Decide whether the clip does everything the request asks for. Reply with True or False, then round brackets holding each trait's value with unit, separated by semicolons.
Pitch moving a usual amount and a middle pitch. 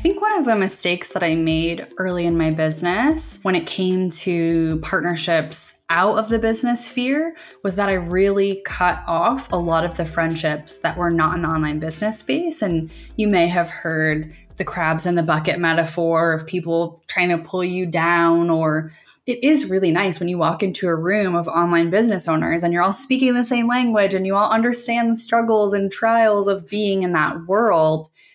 True (4.1 semitones; 180 Hz)